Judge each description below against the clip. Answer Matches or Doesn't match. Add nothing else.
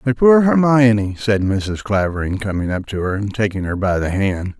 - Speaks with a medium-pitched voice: Doesn't match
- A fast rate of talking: Matches